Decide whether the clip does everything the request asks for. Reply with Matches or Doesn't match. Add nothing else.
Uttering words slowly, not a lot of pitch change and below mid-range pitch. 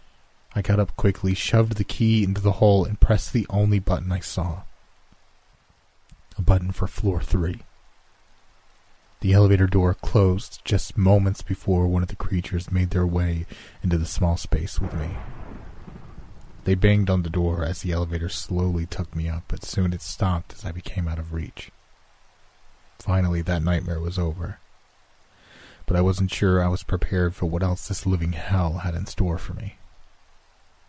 Doesn't match